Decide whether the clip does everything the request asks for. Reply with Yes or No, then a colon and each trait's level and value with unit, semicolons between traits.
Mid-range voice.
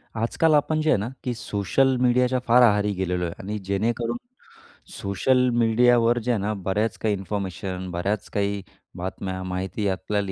No: low, 105 Hz